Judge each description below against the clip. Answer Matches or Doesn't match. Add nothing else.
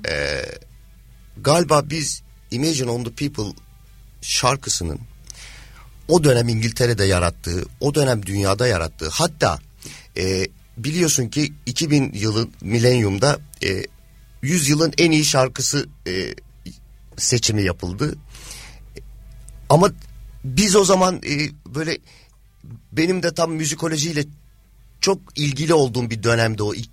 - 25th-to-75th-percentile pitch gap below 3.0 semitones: Doesn't match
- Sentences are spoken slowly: Doesn't match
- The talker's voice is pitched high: Doesn't match